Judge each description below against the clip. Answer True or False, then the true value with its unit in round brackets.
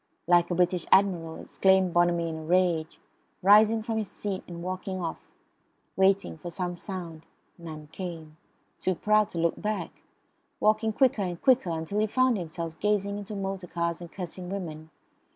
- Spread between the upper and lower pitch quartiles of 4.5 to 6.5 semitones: False (3.1 semitones)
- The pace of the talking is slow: False (165 wpm)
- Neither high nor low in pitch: True (180 Hz)